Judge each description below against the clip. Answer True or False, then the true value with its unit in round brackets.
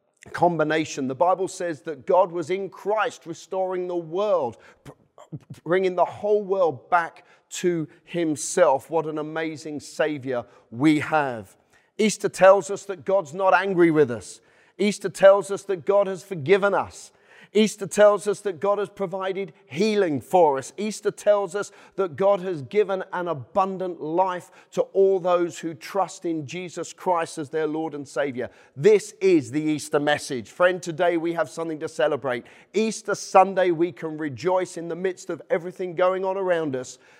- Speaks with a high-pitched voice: False (180 Hz)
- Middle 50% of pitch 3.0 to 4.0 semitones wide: True (3.7 semitones)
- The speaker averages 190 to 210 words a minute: False (165 wpm)